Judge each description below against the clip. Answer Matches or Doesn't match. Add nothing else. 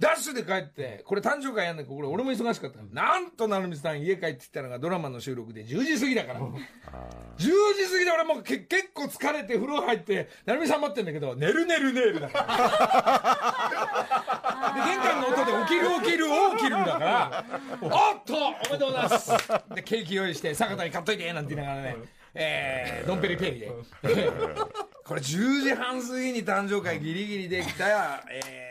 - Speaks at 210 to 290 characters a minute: Doesn't match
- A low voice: Doesn't match